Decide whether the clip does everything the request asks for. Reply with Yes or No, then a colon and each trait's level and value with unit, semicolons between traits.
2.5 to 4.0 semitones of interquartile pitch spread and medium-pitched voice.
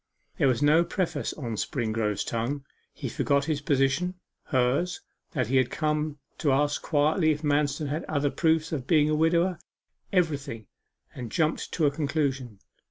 Yes: average, 2.8 semitones; medium, 145 Hz